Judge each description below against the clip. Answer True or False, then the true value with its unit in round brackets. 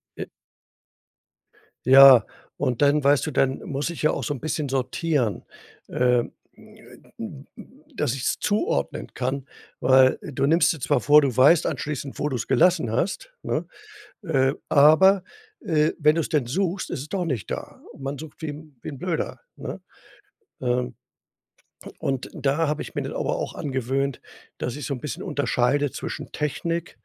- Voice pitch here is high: False (145 Hz)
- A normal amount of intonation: True (3.2 semitones)